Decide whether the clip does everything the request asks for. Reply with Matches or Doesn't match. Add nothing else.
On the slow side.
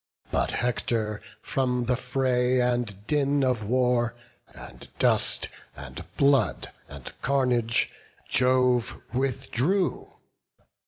Matches